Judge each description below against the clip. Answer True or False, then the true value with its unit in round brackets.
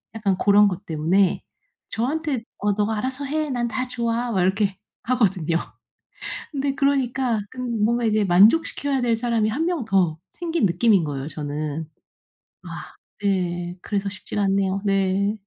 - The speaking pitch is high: True (210 Hz)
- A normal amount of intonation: True (4.8 semitones)